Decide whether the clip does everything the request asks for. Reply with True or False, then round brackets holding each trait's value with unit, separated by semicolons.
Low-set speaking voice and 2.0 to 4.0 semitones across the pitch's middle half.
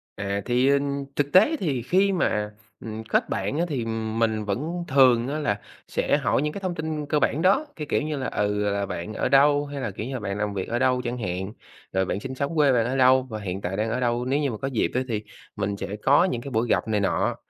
False (125 Hz; 5.3 semitones)